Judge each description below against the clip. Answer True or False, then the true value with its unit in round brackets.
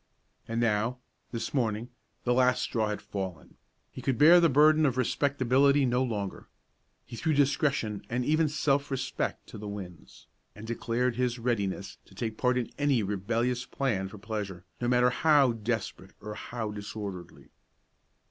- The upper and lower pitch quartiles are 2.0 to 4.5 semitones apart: True (4.1 semitones)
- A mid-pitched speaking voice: False (120 Hz)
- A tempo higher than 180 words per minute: False (155 wpm)